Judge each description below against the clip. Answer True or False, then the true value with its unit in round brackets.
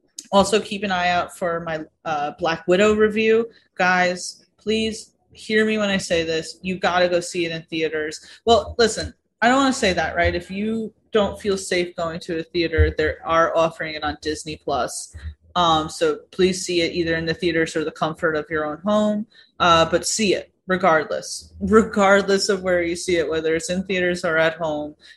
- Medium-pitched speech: True (180 Hz)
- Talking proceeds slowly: False (205 wpm)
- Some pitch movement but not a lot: True (4.1 semitones)